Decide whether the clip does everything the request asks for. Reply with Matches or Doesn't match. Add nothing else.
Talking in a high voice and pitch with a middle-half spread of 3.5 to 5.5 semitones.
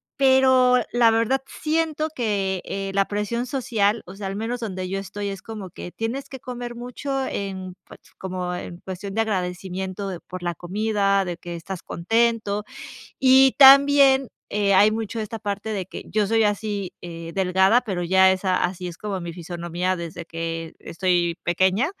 Matches